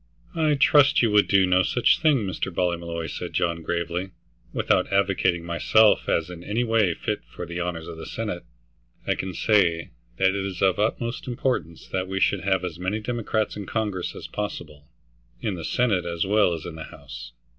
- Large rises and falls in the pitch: No, average, 3.8 semitones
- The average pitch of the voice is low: Yes, very low, 95 Hz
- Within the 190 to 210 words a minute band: Yes, average, 195 wpm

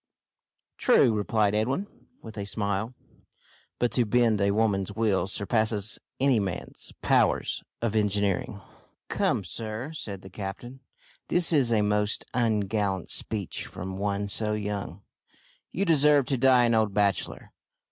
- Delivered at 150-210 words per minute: No, slow, 135 wpm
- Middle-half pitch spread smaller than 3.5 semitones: Yes, average, 2.8 semitones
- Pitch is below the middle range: Yes, low, 105 Hz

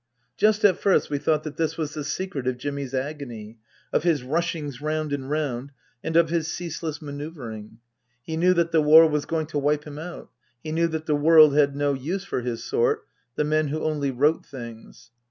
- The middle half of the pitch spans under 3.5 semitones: Yes, narrow, 2.6 semitones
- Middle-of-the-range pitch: Yes, medium, 150 Hz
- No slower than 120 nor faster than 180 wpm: No, fast, 205 wpm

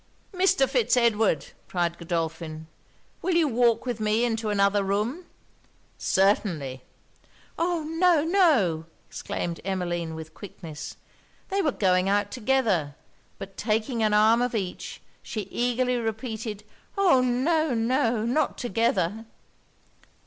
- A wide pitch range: No, average, 5.0 semitones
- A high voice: Yes, high, 225 Hz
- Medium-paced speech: No, slow, 120 wpm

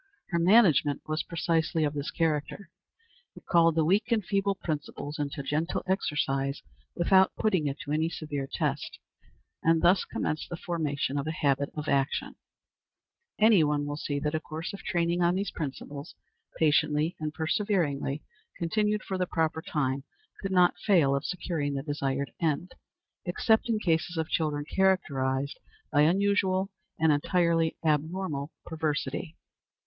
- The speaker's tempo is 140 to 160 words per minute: Yes, average, 150 wpm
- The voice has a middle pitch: Yes, medium, 160 Hz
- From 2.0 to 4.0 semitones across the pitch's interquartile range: Yes, average, 3.6 semitones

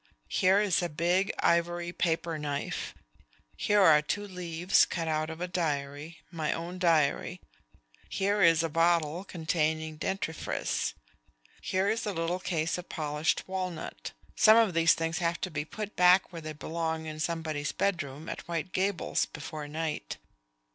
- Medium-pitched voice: Yes, medium, 165 Hz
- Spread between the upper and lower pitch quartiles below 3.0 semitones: Yes, narrow, 2.6 semitones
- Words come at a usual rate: Yes, average, 155 wpm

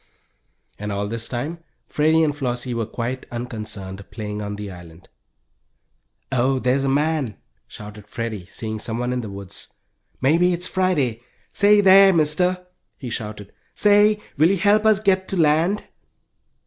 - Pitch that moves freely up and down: Yes, wide, 8.3 semitones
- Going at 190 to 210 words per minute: No, average, 150 wpm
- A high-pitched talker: No, low, 130 Hz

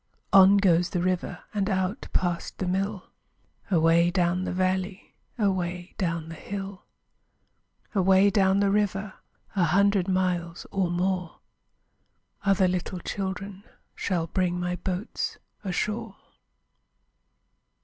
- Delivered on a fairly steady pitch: Yes, narrow, 1.8 semitones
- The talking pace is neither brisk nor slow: No, slow, 115 wpm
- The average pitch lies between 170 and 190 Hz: Yes, medium, 185 Hz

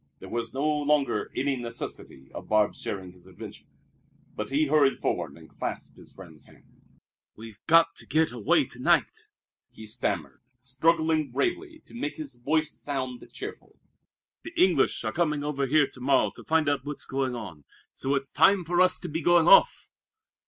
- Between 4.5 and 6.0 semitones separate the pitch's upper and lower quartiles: Yes, average, 4.9 semitones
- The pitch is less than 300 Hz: Yes, medium, 140 Hz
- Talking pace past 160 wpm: Yes, average, 175 wpm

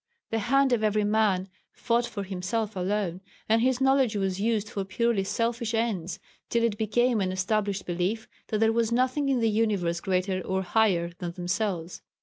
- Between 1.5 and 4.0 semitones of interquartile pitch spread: Yes, average, 3.5 semitones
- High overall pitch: Yes, high, 215 Hz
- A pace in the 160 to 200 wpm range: Yes, average, 175 wpm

